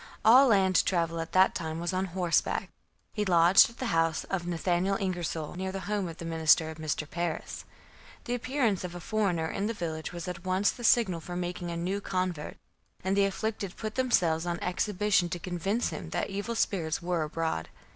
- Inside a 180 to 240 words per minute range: Yes, average, 195 wpm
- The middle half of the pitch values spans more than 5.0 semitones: No, average, 3.0 semitones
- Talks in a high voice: No, medium, 180 Hz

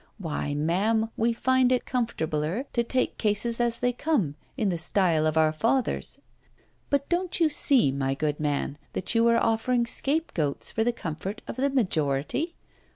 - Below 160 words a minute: No, average, 165 wpm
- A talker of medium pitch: No, high, 225 Hz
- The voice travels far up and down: Yes, wide, 8.1 semitones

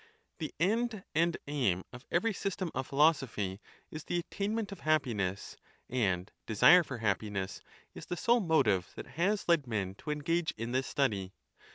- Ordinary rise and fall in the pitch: No, wide, 8.5 semitones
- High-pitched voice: No, medium, 145 Hz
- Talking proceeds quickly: No, average, 165 wpm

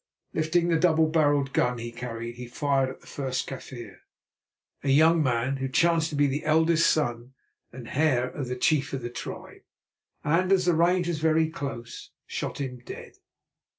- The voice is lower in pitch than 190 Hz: Yes, medium, 140 Hz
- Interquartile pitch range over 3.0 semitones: Yes, average, 4.2 semitones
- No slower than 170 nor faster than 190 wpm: Yes, average, 180 wpm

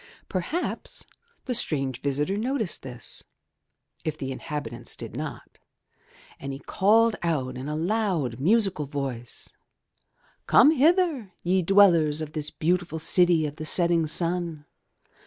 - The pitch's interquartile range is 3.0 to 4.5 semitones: No, average, 5.3 semitones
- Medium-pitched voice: Yes, medium, 165 Hz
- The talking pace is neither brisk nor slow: No, slow, 130 wpm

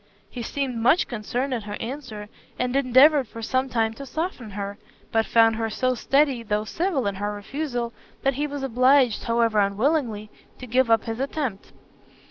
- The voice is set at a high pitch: Yes, high, 240 Hz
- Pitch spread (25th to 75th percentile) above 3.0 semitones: Yes, average, 3.5 semitones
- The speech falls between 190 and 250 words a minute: No, average, 175 wpm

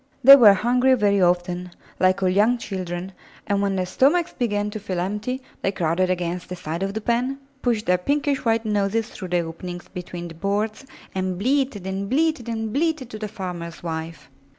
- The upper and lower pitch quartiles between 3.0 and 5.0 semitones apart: Yes, average, 4.7 semitones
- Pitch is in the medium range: No, high, 200 Hz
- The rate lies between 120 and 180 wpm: No, average, 190 wpm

